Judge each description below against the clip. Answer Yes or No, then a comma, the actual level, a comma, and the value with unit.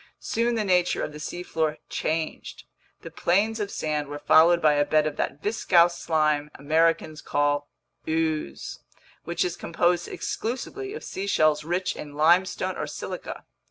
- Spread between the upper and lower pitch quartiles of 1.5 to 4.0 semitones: Yes, average, 3.0 semitones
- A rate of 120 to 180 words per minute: Yes, average, 150 wpm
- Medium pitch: Yes, medium, 165 Hz